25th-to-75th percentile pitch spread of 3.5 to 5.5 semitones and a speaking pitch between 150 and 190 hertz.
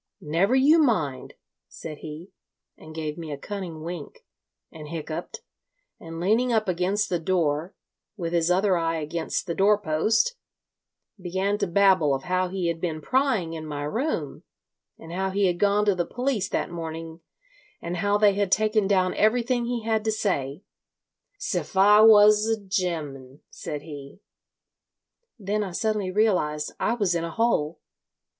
Yes: average, 4.5 semitones; medium, 185 Hz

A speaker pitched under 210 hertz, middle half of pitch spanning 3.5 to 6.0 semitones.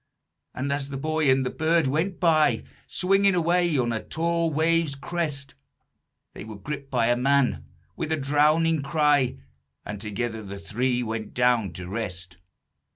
Yes: medium, 140 Hz; average, 5.1 semitones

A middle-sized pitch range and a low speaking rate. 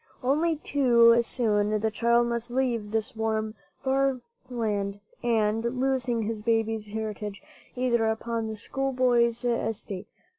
No: narrow, 2.3 semitones; slow, 120 wpm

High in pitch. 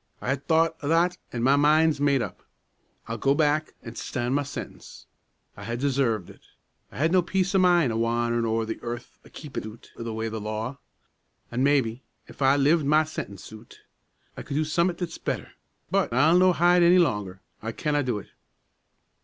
No: medium, 140 Hz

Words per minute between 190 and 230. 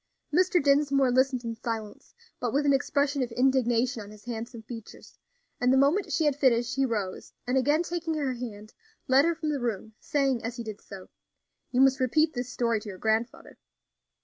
Yes: average, 195 wpm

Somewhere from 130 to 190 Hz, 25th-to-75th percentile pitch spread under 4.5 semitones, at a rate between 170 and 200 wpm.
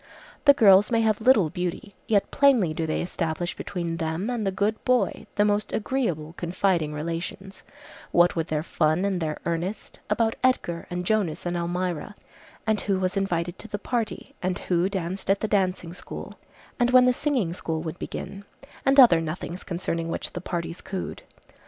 Yes: medium, 185 Hz; average, 3.9 semitones; average, 175 wpm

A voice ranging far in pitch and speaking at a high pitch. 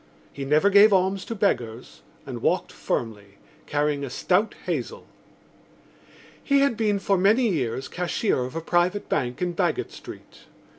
No: wide, 6.8 semitones; medium, 180 Hz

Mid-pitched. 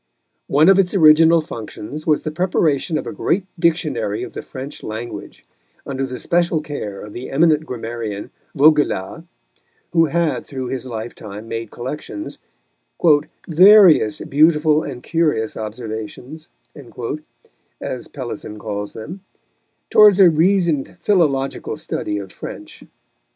Yes: medium, 150 Hz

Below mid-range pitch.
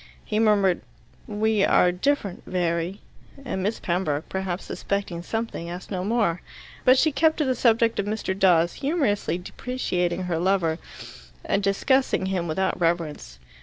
No: high, 190 Hz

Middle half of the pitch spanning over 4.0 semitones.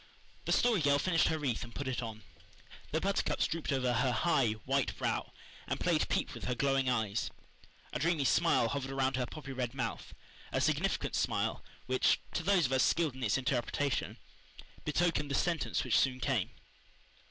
No: average, 3.6 semitones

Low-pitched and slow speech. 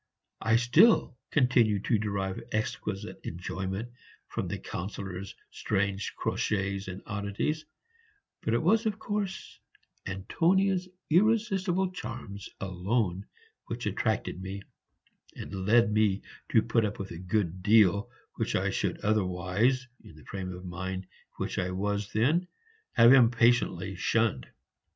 Yes: low, 105 Hz; slow, 125 wpm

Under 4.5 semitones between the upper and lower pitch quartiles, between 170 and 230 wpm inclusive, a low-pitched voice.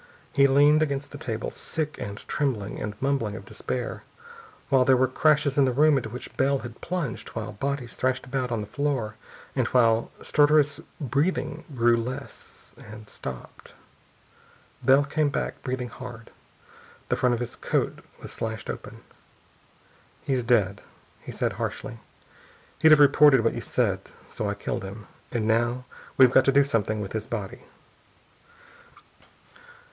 No: average, 3.9 semitones; average, 155 wpm; low, 130 Hz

